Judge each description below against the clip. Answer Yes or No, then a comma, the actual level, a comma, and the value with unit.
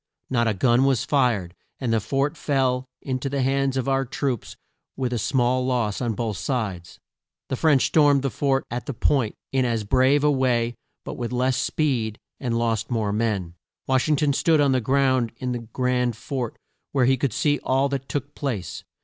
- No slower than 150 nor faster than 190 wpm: No, average, 200 wpm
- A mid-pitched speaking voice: No, low, 130 Hz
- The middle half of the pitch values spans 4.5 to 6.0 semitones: No, average, 2.7 semitones